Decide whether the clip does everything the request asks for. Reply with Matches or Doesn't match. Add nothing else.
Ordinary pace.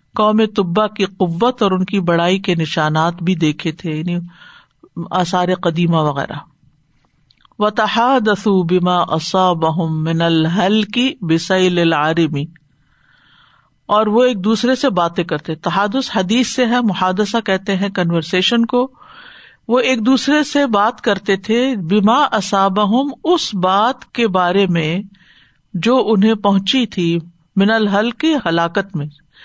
Matches